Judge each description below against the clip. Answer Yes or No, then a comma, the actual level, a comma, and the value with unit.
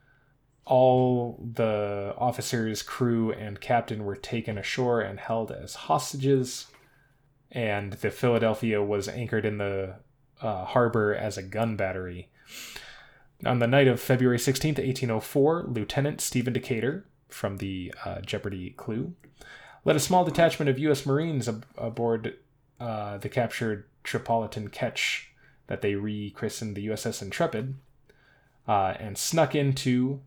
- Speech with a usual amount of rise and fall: Yes, average, 4.2 semitones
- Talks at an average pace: No, slow, 130 wpm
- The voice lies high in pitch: No, low, 120 Hz